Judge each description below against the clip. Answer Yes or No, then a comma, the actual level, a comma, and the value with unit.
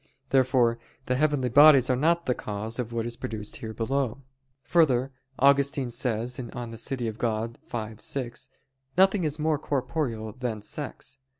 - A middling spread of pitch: Yes, average, 3.3 semitones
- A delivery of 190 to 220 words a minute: No, average, 160 wpm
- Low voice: Yes, low, 125 Hz